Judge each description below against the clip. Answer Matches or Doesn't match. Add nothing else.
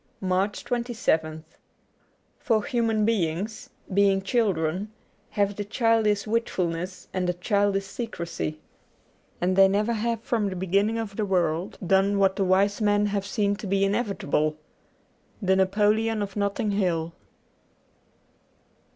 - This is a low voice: Doesn't match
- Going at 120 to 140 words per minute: Matches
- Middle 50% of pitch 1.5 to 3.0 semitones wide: Matches